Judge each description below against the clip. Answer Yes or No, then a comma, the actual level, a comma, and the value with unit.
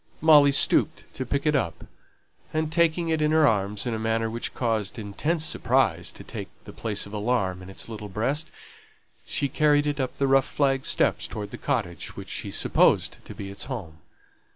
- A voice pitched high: No, low, 125 Hz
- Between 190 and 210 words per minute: Yes, average, 195 wpm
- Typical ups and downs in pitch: No, wide, 6.0 semitones